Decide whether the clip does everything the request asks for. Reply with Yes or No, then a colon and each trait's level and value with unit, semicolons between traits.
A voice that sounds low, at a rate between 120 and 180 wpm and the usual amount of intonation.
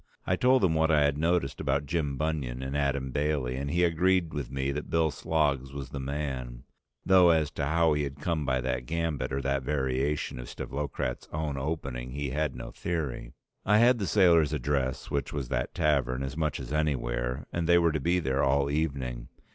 No: very low, 70 Hz; fast, 205 wpm; average, 3.2 semitones